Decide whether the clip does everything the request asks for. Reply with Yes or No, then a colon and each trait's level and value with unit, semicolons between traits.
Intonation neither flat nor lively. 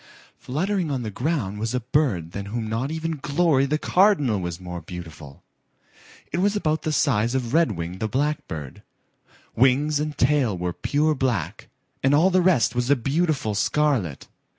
No: wide, 6.7 semitones